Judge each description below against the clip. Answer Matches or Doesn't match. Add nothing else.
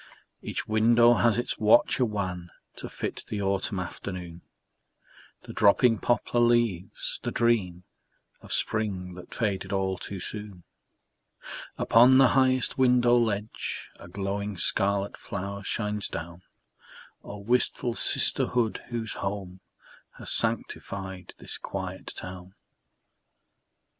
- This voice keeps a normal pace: Doesn't match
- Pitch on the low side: Matches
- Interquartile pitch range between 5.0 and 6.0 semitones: Doesn't match